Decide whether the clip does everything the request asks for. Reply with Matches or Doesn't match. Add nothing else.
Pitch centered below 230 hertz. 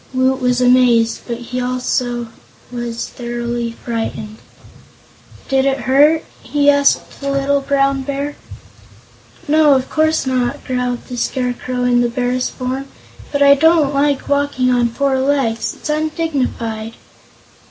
Doesn't match